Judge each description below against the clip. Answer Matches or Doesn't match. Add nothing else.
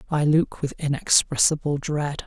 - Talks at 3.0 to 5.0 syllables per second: Matches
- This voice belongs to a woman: Doesn't match